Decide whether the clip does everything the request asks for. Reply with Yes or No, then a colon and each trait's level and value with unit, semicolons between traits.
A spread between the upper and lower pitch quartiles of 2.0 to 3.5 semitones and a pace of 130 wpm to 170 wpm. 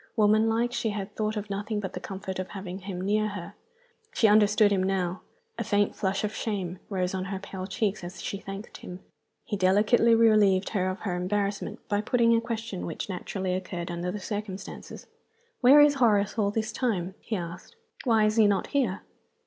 No: narrow, 2.5 semitones; average, 195 wpm